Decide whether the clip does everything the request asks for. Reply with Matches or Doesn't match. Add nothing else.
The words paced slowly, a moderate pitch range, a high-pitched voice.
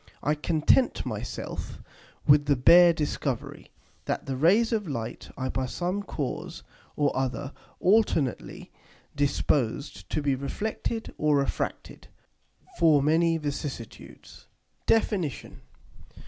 Doesn't match